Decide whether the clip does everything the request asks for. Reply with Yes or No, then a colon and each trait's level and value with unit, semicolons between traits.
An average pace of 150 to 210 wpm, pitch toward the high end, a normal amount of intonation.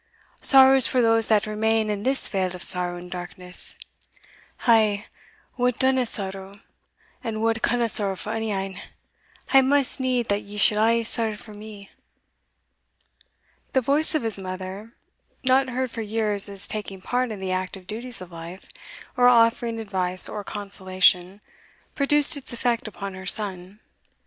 Yes: average, 155 wpm; high, 215 Hz; average, 3.9 semitones